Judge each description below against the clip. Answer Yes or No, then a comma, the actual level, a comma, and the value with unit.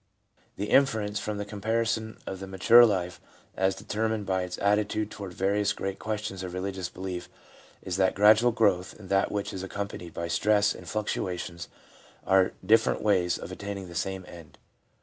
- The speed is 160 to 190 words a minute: Yes, average, 170 wpm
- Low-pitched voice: Yes, low, 100 Hz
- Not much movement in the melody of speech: Yes, narrow, 2.2 semitones